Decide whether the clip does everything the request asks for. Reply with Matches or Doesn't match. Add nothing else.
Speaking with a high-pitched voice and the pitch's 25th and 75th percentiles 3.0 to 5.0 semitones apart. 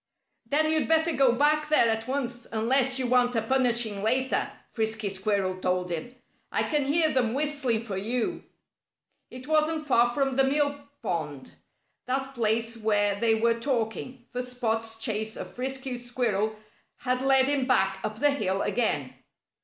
Matches